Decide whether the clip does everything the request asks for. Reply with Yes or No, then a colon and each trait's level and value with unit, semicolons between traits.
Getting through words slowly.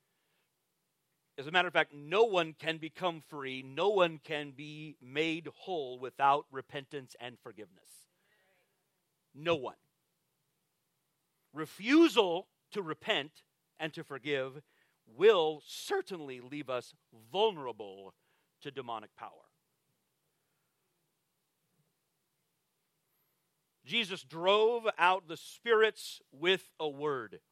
Yes: slow, 95 wpm